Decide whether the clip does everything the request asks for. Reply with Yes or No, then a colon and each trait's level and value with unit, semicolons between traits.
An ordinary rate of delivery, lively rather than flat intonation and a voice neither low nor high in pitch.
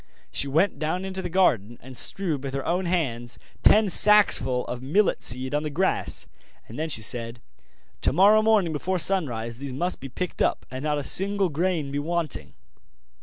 Yes: average, 175 wpm; wide, 6.2 semitones; medium, 155 Hz